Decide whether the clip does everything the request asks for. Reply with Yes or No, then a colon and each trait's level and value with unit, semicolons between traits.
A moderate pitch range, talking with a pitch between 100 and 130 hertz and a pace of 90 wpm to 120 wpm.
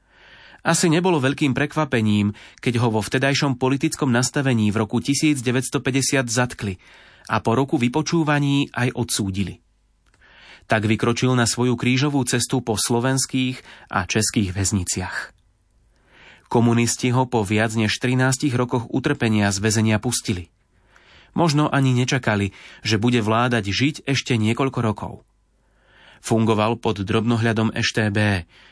Yes: average, 3.4 semitones; low, 120 Hz; average, 115 wpm